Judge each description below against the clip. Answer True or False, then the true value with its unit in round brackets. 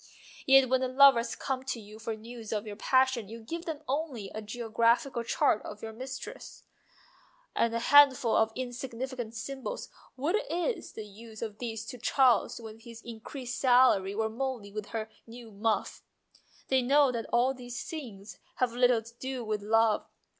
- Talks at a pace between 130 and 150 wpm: False (175 wpm)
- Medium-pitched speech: False (235 Hz)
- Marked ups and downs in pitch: False (2.9 semitones)